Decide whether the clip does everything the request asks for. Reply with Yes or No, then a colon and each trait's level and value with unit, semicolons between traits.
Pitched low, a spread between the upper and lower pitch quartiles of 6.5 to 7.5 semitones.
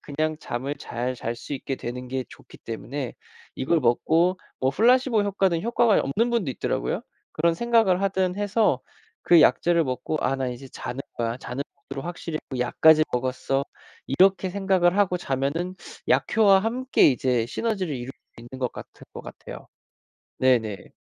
No: medium, 155 Hz; wide, 6.9 semitones